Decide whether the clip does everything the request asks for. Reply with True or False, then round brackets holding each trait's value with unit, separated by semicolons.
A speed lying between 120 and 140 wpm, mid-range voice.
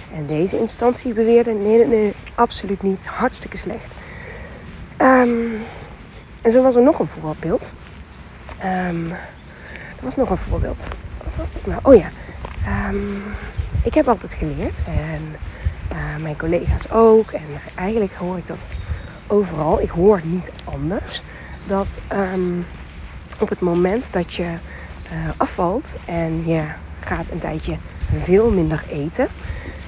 True (135 wpm; 165 Hz)